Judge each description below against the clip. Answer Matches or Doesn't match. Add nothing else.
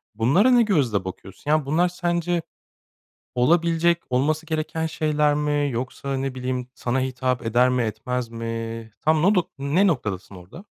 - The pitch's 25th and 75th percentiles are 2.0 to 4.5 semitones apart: Doesn't match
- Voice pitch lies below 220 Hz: Matches